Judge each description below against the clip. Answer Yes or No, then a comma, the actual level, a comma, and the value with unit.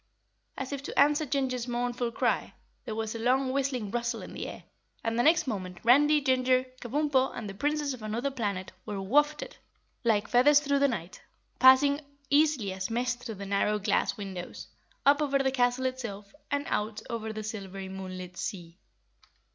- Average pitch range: Yes, average, 4.7 semitones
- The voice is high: Yes, high, 245 Hz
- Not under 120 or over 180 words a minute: Yes, average, 170 wpm